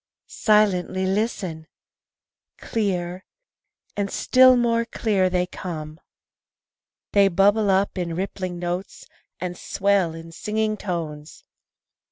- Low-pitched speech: No, high, 190 Hz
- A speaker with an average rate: No, slow, 100 wpm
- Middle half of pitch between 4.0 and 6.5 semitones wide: No, average, 3.1 semitones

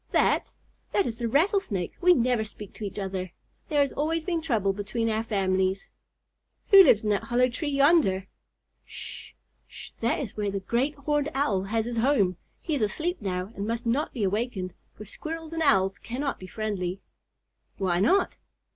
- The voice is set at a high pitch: Yes, high, 230 Hz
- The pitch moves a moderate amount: No, wide, 6.7 semitones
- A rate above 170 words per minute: Yes, average, 180 wpm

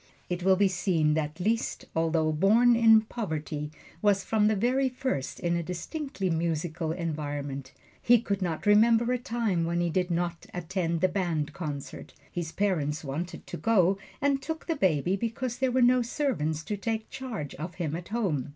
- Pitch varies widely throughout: Yes, wide, 5.9 semitones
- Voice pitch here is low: No, medium, 180 Hz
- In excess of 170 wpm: Yes, average, 180 wpm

